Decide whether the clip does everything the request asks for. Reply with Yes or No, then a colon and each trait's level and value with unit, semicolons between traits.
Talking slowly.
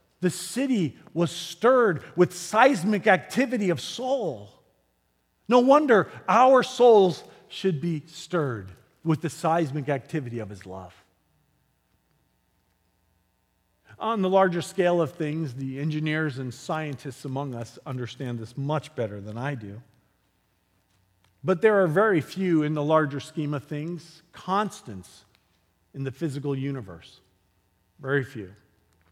Yes: slow, 125 wpm